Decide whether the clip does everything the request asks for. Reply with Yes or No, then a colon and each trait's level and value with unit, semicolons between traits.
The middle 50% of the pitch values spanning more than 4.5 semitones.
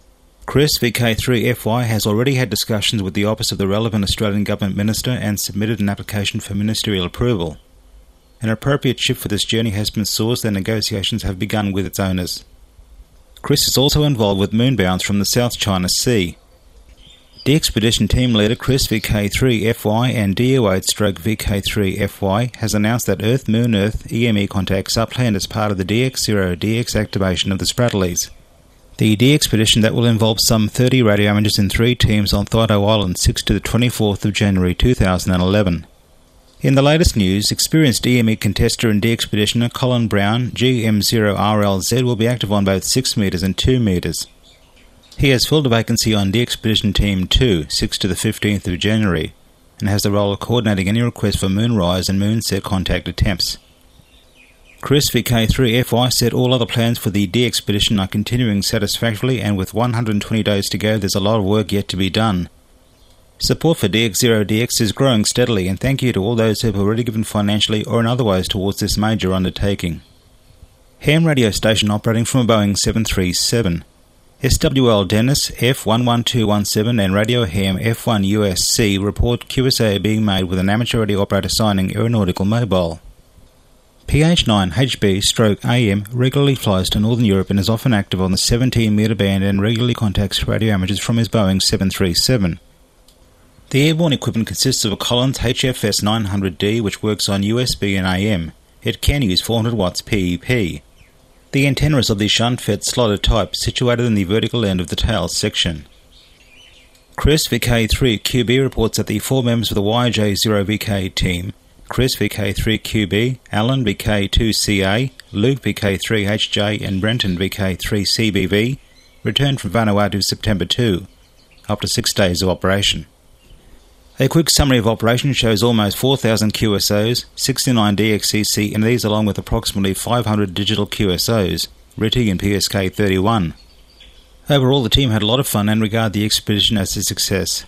No: average, 3.4 semitones